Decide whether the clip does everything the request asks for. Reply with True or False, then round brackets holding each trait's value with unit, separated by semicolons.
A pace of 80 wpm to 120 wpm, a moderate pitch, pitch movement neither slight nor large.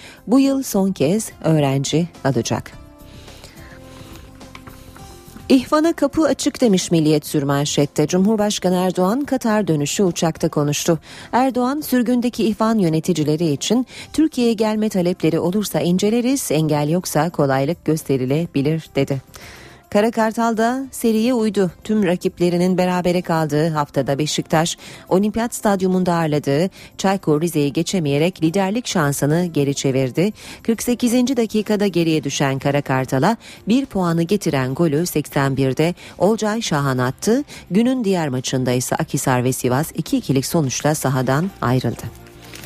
False (110 wpm; 170 Hz; 6.8 semitones)